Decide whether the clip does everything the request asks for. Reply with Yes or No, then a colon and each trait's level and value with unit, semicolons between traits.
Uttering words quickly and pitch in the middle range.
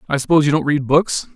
Yes: fast, 265 wpm; medium, 145 Hz